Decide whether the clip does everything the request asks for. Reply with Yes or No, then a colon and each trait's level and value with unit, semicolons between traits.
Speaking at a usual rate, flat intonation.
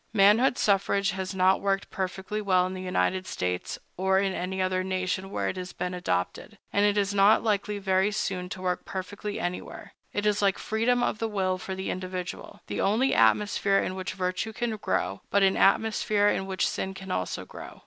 Yes: average, 195 wpm; narrow, 1.8 semitones